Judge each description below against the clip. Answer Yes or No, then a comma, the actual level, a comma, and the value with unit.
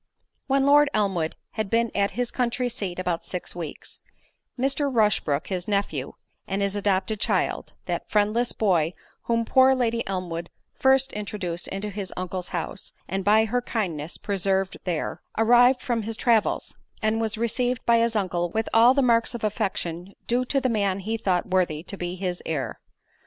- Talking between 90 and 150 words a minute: No, average, 165 wpm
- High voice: Yes, high, 210 Hz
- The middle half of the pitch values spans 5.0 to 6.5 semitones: No, average, 4.3 semitones